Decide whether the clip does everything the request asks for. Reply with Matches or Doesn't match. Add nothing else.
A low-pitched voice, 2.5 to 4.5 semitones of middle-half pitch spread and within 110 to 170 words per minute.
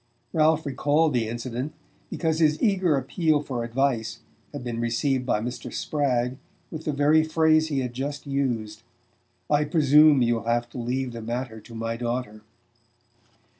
Matches